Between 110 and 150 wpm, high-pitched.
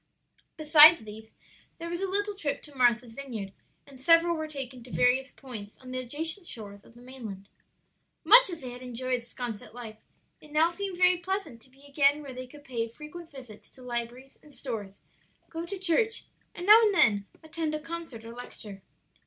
No: average, 190 wpm; very high, 270 Hz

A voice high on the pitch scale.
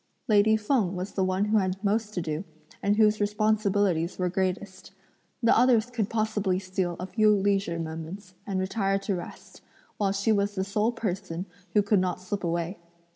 Yes: high, 200 Hz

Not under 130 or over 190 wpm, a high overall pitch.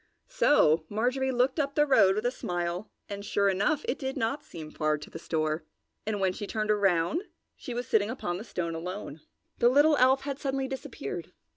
No: average, 200 wpm; high, 215 Hz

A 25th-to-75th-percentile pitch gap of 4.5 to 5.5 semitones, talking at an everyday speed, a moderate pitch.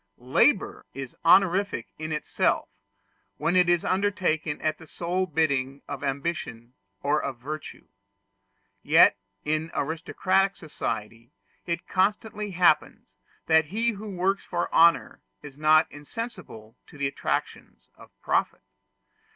No: average, 4.8 semitones; slow, 120 wpm; medium, 160 Hz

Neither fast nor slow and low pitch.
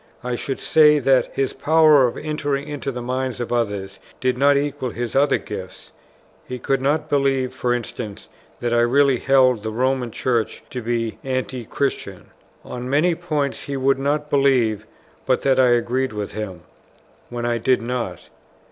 Yes: average, 170 wpm; low, 130 Hz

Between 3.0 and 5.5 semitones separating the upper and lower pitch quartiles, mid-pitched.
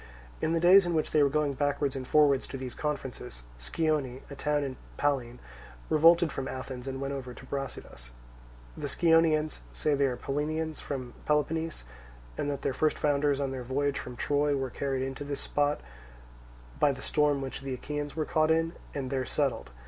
No: narrow, 2.4 semitones; medium, 145 Hz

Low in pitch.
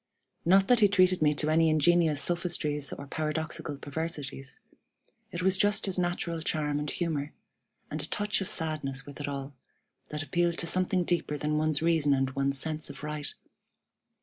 No: medium, 155 Hz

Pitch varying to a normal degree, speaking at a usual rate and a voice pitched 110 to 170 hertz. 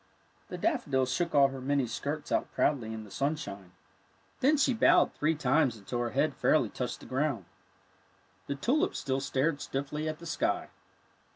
Yes: average, 3.4 semitones; average, 170 wpm; medium, 140 Hz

